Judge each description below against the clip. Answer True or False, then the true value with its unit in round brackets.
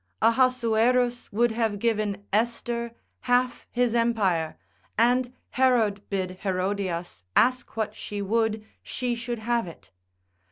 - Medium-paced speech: False (115 wpm)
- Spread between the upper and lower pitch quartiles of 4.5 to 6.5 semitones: False (2.9 semitones)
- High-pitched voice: True (230 Hz)